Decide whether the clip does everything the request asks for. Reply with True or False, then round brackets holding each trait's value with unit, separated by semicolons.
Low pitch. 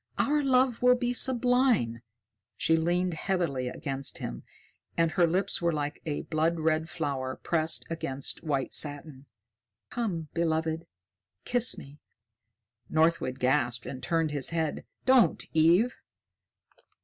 False (160 Hz)